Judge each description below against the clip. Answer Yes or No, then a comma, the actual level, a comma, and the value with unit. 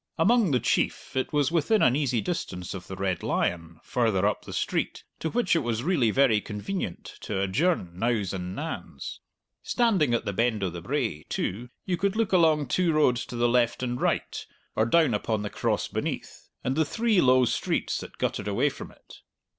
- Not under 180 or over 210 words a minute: Yes, average, 195 wpm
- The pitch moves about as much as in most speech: No, wide, 7.8 semitones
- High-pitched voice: No, low, 125 Hz